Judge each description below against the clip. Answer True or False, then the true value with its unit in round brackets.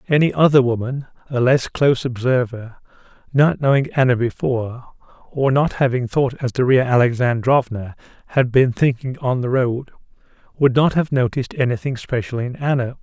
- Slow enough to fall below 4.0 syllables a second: False (5.3 syllables/s)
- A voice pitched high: False (130 Hz)